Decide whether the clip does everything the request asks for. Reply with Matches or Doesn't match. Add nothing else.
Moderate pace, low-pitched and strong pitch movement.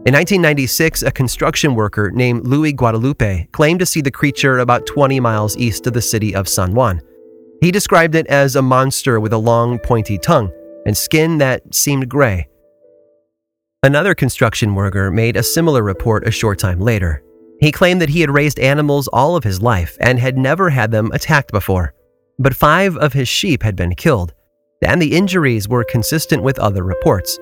Matches